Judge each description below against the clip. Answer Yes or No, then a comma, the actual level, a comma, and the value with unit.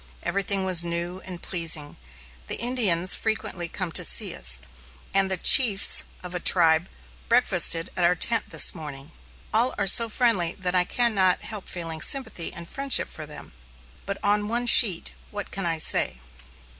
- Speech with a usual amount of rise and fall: Yes, average, 3.8 semitones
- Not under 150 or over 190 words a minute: Yes, average, 170 wpm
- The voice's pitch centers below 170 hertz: No, medium, 185 Hz